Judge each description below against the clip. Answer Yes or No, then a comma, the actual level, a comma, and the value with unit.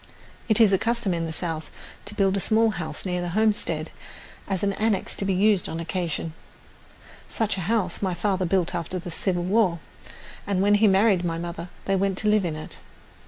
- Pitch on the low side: No, high, 190 Hz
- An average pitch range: Yes, average, 3.1 semitones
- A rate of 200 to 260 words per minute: Yes, fast, 205 wpm